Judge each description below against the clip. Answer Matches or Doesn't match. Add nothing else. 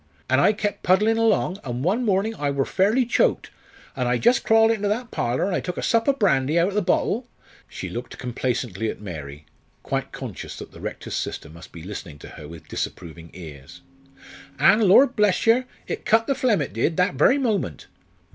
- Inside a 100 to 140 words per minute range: Doesn't match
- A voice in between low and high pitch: Matches